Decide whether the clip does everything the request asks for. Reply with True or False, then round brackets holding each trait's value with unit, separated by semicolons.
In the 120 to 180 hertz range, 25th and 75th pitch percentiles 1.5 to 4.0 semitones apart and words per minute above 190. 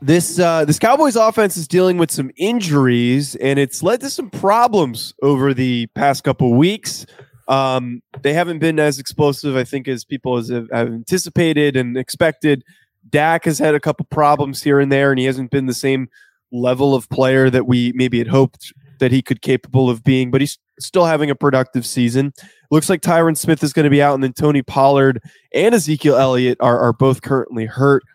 True (140 Hz; 3.4 semitones; 200 wpm)